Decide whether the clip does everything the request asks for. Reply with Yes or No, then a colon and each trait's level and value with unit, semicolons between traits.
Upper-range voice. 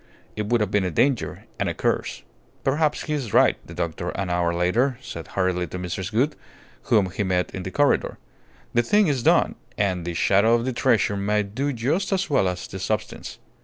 No: low, 105 Hz